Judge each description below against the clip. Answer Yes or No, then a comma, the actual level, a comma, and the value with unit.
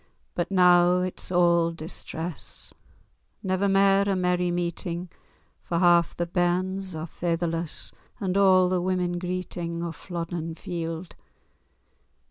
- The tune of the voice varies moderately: No, narrow, 1.4 semitones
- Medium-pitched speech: Yes, medium, 175 Hz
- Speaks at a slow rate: Yes, slow, 120 wpm